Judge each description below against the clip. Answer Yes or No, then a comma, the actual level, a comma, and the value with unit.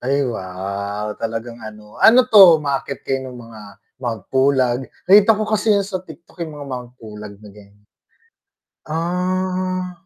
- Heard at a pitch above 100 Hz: Yes, low, 135 Hz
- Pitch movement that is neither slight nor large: No, wide, 9.0 semitones